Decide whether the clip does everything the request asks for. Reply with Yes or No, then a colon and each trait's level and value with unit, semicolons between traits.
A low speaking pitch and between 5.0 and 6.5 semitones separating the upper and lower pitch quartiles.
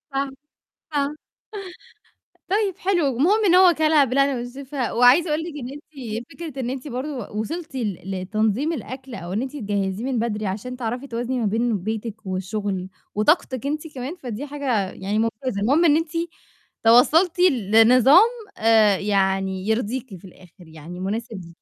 No: high, 245 Hz; wide, 5.4 semitones